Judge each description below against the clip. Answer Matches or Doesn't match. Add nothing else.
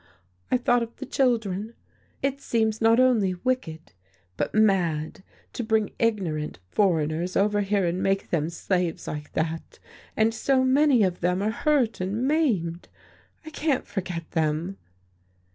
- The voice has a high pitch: Matches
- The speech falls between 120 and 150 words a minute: Matches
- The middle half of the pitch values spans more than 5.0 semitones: Matches